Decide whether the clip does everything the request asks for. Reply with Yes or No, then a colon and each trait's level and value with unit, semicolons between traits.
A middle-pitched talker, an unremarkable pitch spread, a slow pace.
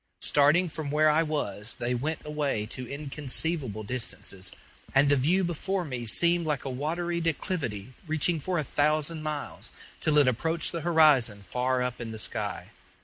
No: medium, 145 Hz; average, 4.4 semitones; average, 165 wpm